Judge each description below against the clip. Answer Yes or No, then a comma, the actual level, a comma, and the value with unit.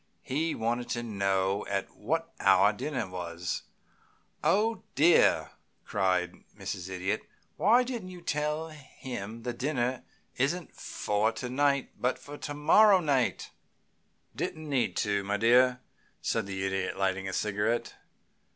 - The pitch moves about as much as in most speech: No, wide, 7.1 semitones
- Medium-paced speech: No, slow, 130 wpm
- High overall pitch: No, low, 120 Hz